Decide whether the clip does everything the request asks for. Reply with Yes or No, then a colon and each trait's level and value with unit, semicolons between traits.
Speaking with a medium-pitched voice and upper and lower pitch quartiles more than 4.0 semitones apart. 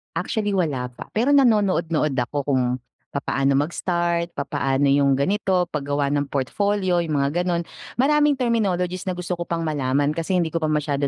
Yes: medium, 165 Hz; average, 4.7 semitones